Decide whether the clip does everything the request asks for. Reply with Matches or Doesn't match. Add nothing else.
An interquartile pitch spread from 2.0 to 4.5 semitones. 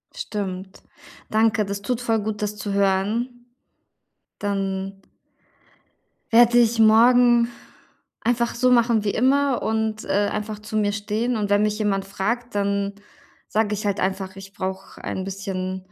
Matches